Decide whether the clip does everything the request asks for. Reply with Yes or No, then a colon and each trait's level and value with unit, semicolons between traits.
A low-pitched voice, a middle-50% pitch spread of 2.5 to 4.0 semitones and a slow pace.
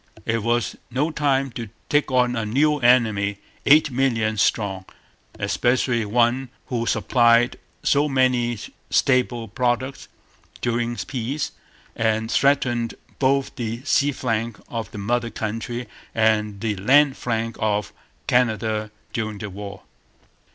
Yes: low, 120 Hz; average, 2.8 semitones; slow, 120 wpm